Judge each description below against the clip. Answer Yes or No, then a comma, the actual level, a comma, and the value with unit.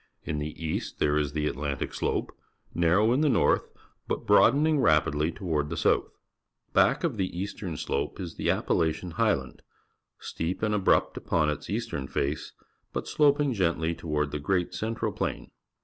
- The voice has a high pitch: No, very low, 85 Hz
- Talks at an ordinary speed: Yes, average, 165 wpm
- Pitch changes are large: Yes, wide, 5.8 semitones